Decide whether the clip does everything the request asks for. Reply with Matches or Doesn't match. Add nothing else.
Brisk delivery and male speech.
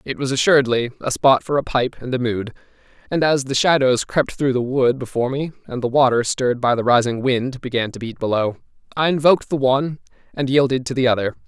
Matches